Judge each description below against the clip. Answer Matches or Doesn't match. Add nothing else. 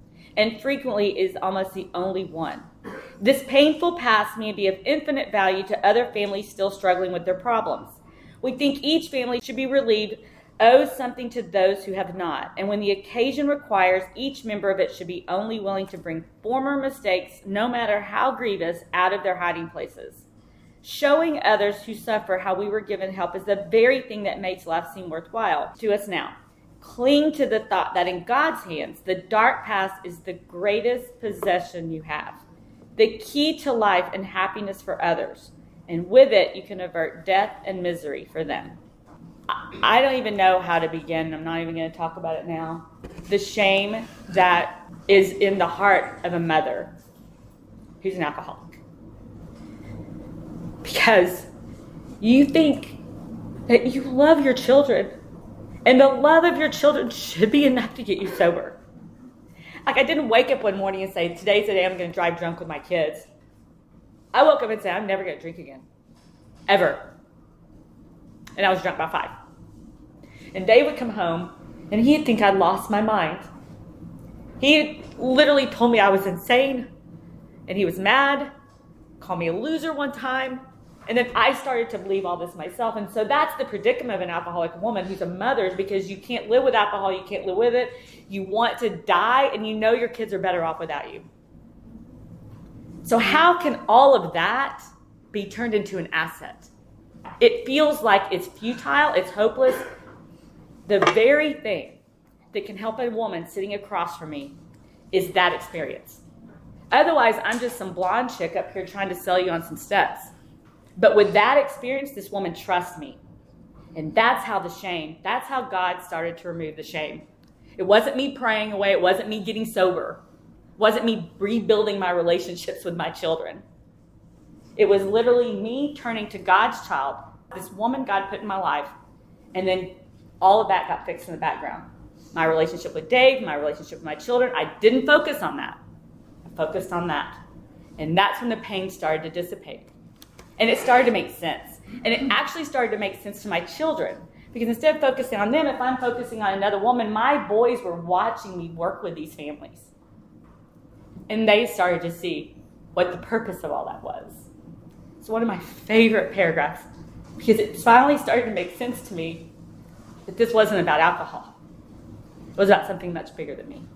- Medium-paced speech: Matches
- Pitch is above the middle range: Matches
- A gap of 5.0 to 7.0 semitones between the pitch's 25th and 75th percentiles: Matches